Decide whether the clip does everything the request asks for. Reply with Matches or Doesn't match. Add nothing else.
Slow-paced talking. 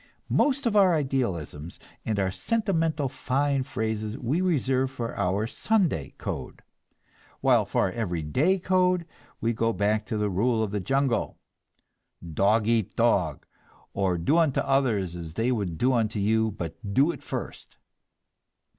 Doesn't match